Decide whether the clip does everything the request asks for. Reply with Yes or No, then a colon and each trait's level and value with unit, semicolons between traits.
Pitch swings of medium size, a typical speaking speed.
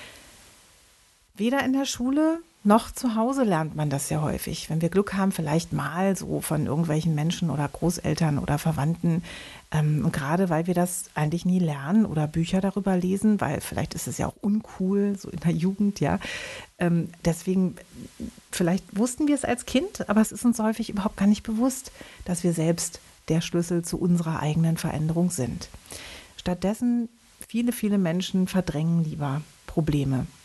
Yes: average, 4.2 semitones; average, 165 wpm